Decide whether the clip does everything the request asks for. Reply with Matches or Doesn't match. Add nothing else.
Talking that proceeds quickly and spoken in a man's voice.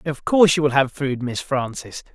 Matches